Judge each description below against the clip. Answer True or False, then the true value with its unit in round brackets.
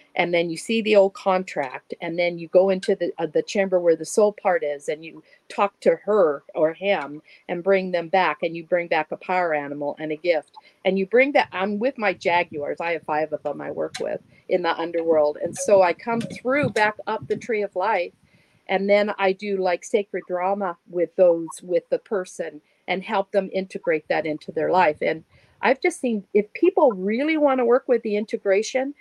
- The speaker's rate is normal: False (215 wpm)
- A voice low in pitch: False (190 Hz)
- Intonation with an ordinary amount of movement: True (3.9 semitones)